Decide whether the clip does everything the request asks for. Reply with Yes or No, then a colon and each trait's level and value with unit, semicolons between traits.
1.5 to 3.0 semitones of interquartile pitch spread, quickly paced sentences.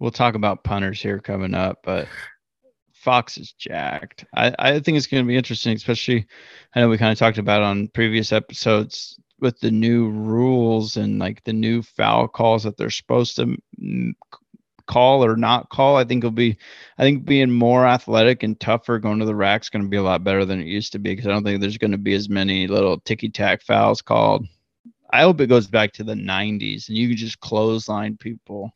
Yes: average, 2.7 semitones; fast, 210 wpm